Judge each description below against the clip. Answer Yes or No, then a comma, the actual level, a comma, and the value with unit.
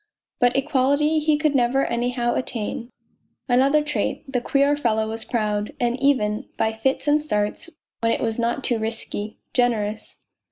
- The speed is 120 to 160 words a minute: Yes, average, 155 wpm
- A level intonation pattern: No, average, 3.8 semitones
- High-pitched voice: Yes, high, 245 Hz